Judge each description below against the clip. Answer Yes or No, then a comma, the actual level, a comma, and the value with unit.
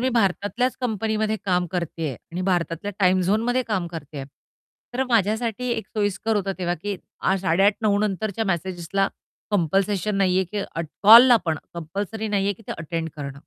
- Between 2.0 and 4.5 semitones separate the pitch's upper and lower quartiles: Yes, average, 3.6 semitones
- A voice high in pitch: Yes, high, 195 Hz